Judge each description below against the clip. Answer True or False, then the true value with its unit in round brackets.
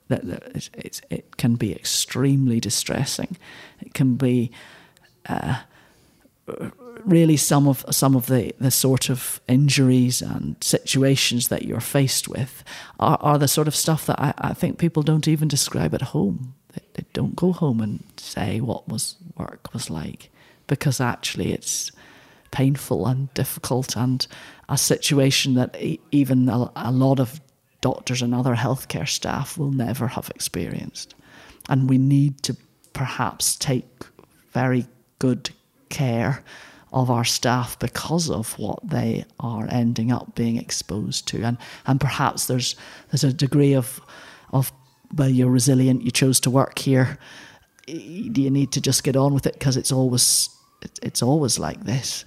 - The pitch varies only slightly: True (2.2 semitones)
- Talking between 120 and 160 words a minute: True (155 wpm)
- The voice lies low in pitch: True (130 Hz)